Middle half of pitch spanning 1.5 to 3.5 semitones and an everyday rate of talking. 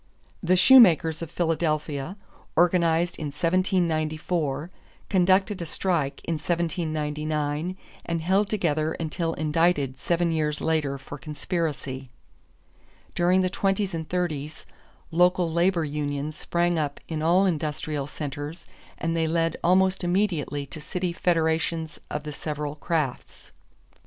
No: average, 2.7 semitones; slow, 120 wpm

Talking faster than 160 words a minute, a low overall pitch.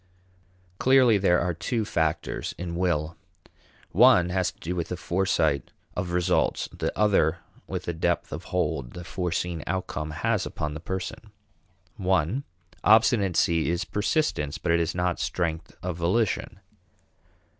No: average, 140 wpm; very low, 90 Hz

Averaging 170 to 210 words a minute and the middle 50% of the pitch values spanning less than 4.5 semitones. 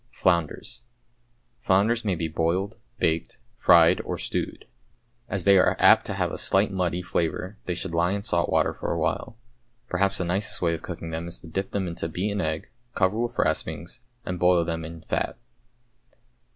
Yes: average, 180 wpm; average, 2.7 semitones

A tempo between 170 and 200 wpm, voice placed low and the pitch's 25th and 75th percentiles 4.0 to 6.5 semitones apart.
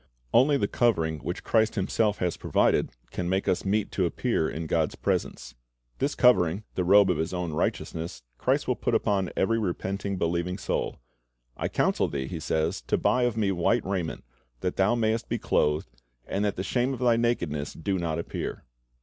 Yes: average, 185 wpm; very low, 95 Hz; average, 4.7 semitones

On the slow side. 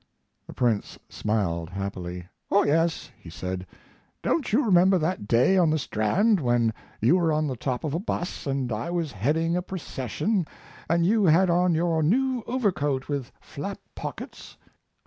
No: average, 165 wpm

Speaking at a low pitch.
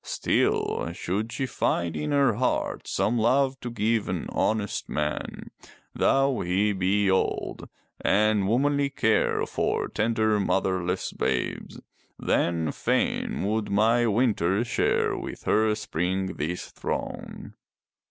Yes: low, 105 Hz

